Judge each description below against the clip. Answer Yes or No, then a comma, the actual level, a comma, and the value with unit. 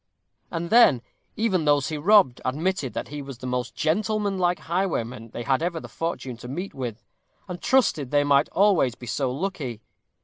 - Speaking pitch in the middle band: Yes, medium, 150 Hz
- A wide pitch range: Yes, wide, 6.3 semitones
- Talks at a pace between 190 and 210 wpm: No, average, 175 wpm